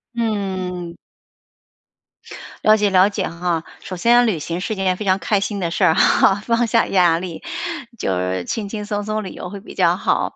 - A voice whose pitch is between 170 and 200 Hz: Yes, high, 195 Hz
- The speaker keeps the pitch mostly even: No, average, 3.1 semitones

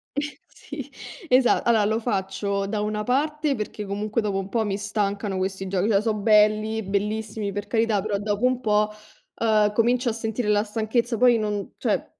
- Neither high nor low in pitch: No, high, 215 Hz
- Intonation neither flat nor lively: No, narrow, 2.0 semitones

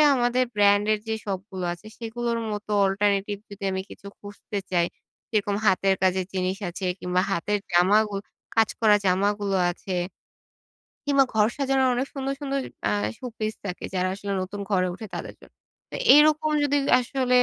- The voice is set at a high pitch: Yes, high, 205 Hz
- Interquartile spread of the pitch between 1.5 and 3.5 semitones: No, average, 3.9 semitones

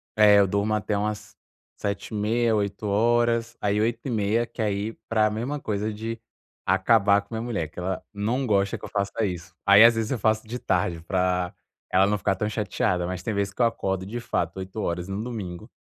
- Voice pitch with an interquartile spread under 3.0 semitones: Yes, narrow, 2.6 semitones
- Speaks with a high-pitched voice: No, low, 105 Hz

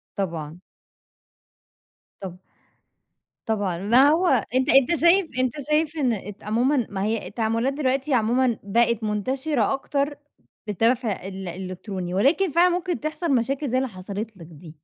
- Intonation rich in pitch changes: Yes, wide, 5.7 semitones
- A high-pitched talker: Yes, high, 235 Hz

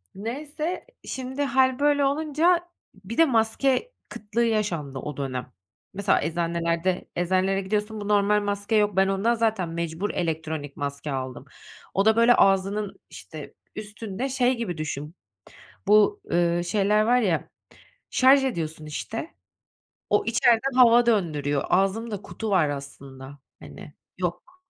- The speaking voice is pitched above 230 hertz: No, high, 205 Hz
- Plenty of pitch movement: Yes, wide, 5.9 semitones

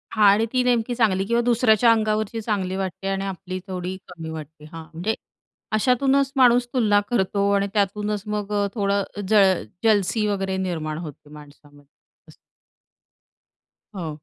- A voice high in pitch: Yes, high, 200 Hz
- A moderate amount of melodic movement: Yes, average, 3.2 semitones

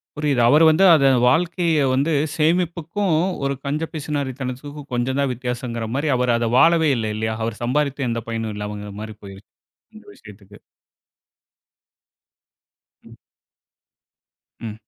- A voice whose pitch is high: No, low, 135 Hz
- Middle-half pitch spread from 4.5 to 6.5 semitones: Yes, average, 4.9 semitones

